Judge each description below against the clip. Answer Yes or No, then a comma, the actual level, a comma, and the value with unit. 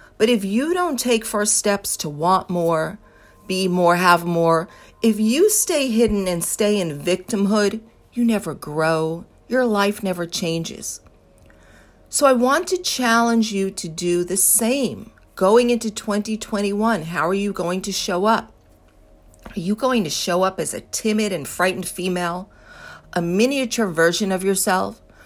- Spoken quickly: No, average, 155 wpm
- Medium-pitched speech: No, high, 195 Hz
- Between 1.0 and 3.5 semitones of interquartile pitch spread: No, average, 4.6 semitones